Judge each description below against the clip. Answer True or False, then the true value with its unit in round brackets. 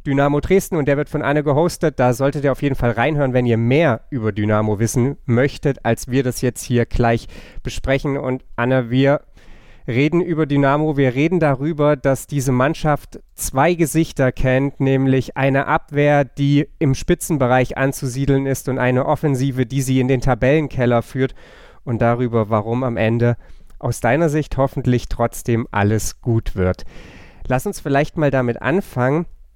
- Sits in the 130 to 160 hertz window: True (135 Hz)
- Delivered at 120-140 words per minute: False (160 wpm)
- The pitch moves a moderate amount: True (3.2 semitones)